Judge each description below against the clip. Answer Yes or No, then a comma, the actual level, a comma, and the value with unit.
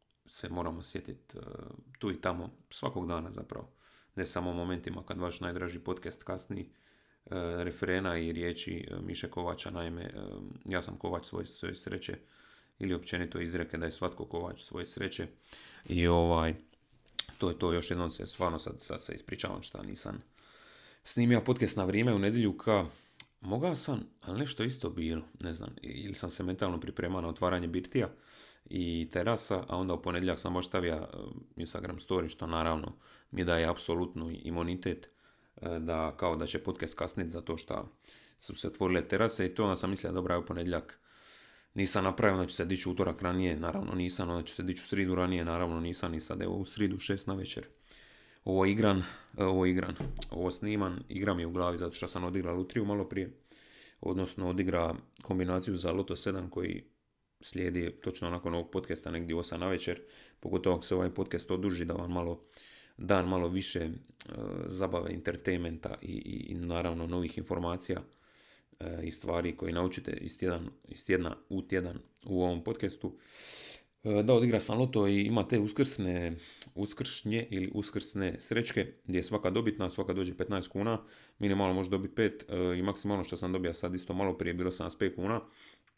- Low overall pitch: Yes, very low, 90 Hz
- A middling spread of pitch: No, narrow, 2.2 semitones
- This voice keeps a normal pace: No, fast, 170 wpm